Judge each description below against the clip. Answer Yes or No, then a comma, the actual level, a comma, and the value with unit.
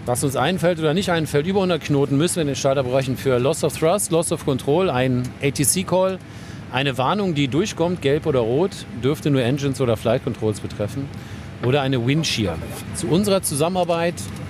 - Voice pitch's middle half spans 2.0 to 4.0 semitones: No, average, 5.0 semitones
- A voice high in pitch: No, medium, 140 Hz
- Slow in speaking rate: No, average, 180 wpm